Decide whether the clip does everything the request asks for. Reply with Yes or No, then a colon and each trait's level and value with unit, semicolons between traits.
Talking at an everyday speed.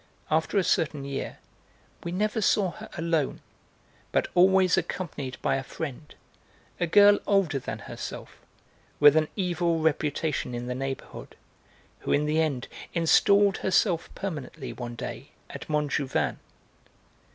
No: slow, 130 wpm